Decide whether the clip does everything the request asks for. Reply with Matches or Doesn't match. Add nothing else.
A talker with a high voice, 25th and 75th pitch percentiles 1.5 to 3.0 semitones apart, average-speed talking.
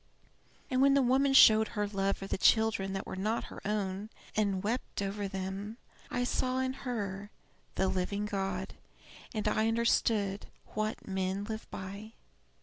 Matches